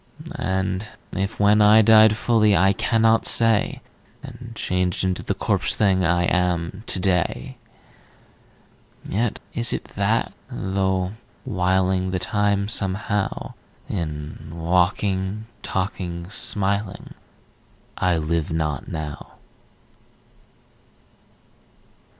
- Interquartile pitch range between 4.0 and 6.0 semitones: No, narrow, 2.5 semitones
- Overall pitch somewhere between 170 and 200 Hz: No, very low, 95 Hz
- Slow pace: Yes, slow, 95 wpm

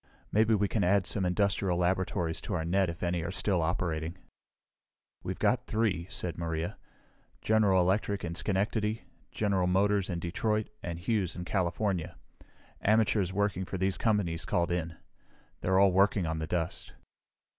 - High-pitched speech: No, very low, 95 Hz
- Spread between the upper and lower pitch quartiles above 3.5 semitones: No, average, 3.0 semitones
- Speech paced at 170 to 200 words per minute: No, average, 155 wpm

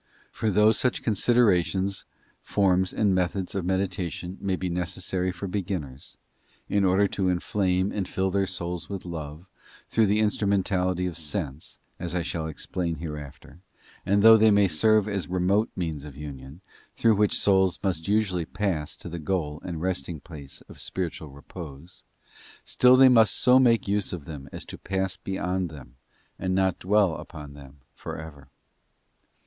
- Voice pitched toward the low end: Yes, very low, 90 Hz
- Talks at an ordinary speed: Yes, average, 160 wpm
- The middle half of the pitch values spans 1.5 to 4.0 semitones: Yes, average, 3.6 semitones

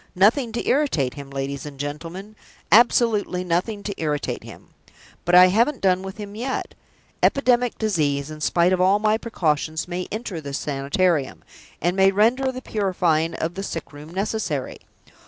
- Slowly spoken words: No, average, 160 wpm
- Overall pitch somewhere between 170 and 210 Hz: Yes, medium, 185 Hz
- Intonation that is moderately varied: No, wide, 5.8 semitones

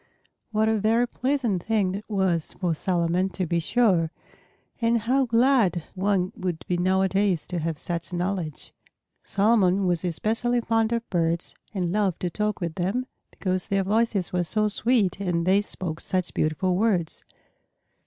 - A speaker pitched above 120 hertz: Yes, high, 190 Hz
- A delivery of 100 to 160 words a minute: Yes, average, 155 wpm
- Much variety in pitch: No, average, 3.8 semitones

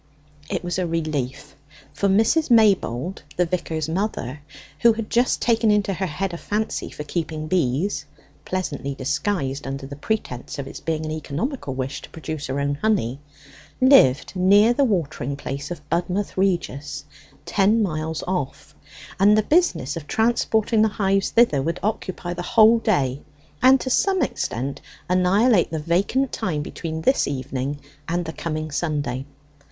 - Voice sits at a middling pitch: Yes, medium, 175 Hz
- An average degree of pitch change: No, wide, 6.5 semitones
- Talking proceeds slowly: No, average, 155 wpm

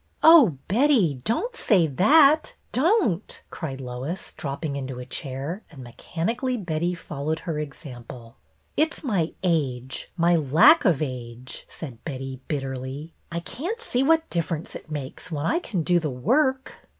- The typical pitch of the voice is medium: Yes, medium, 165 Hz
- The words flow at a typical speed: Yes, average, 160 wpm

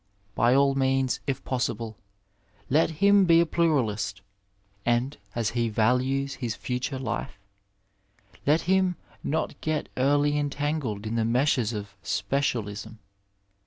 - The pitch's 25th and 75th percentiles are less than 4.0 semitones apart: No, average, 4.5 semitones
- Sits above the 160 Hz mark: No, low, 130 Hz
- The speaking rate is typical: No, slow, 130 wpm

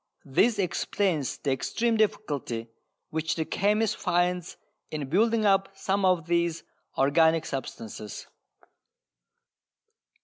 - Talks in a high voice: No, medium, 170 Hz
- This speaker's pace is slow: Yes, slow, 100 wpm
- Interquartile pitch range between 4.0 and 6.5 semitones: Yes, average, 5.1 semitones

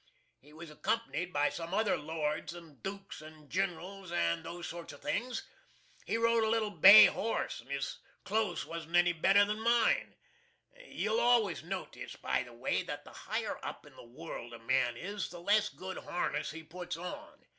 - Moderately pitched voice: Yes, medium, 175 Hz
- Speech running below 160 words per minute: No, average, 180 wpm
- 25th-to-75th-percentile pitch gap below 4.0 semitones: No, average, 4.6 semitones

